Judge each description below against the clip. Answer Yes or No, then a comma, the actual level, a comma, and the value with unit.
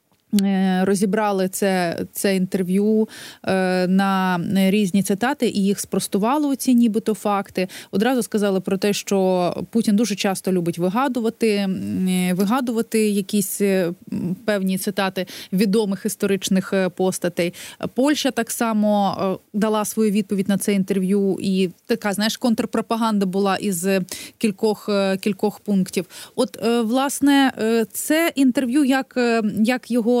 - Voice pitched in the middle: No, high, 205 Hz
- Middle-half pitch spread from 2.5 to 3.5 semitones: Yes, average, 3.0 semitones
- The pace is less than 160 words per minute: Yes, average, 110 wpm